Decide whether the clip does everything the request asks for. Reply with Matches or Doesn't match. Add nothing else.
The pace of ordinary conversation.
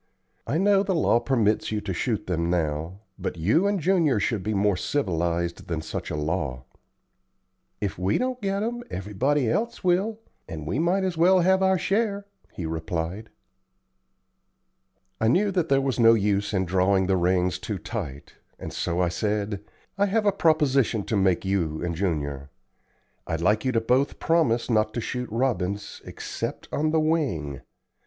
Matches